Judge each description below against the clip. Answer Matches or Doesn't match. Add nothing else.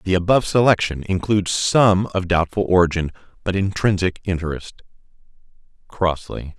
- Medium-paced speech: Doesn't match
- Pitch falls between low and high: Doesn't match